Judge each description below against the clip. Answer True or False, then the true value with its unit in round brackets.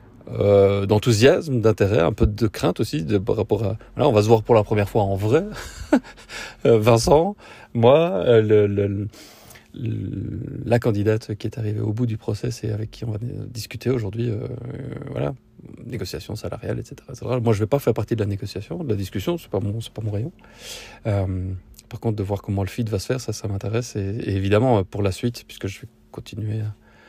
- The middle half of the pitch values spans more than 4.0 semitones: False (2.7 semitones)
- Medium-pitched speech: False (110 Hz)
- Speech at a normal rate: True (210 wpm)